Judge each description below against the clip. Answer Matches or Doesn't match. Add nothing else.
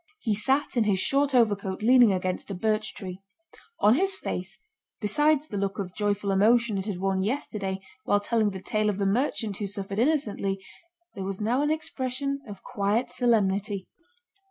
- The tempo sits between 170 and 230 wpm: Matches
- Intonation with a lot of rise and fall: Doesn't match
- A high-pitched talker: Matches